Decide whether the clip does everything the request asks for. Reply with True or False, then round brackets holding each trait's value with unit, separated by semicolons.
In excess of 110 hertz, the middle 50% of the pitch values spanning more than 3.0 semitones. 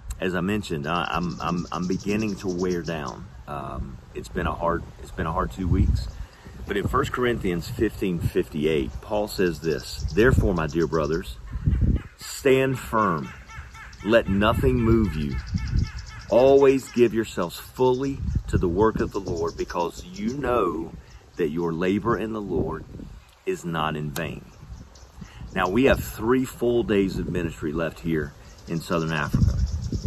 False (90 Hz; 5.2 semitones)